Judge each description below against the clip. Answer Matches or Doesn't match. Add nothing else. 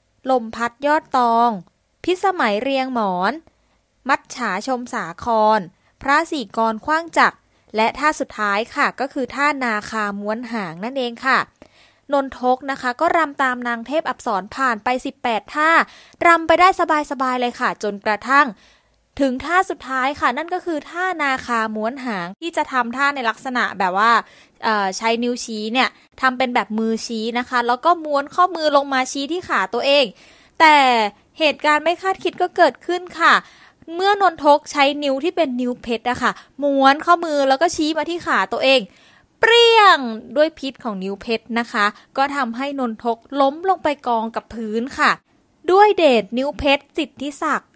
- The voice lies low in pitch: Doesn't match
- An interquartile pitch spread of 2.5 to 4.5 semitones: Doesn't match